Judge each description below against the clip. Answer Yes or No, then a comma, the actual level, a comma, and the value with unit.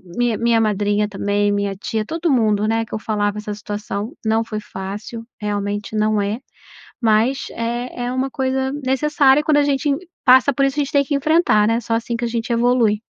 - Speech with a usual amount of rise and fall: Yes, average, 4.0 semitones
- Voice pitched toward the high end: Yes, high, 230 Hz